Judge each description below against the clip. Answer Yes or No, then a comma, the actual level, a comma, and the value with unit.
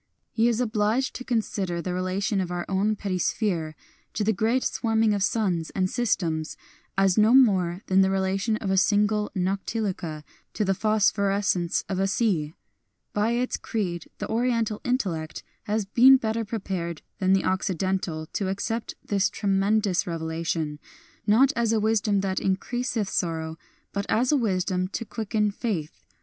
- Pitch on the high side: Yes, high, 200 Hz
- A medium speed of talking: Yes, average, 155 wpm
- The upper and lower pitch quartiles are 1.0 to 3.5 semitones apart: Yes, average, 3.1 semitones